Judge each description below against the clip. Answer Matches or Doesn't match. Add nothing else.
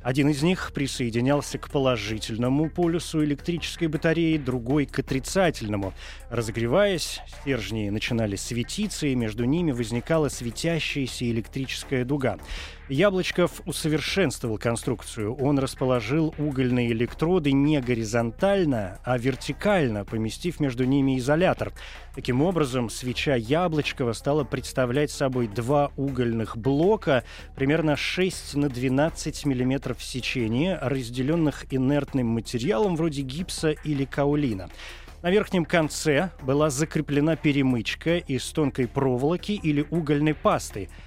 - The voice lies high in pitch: Doesn't match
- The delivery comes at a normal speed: Doesn't match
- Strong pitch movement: Doesn't match